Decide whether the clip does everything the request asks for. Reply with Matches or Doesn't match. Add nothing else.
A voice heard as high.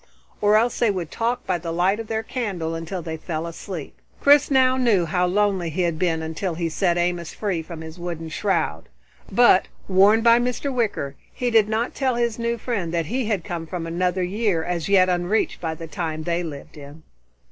Doesn't match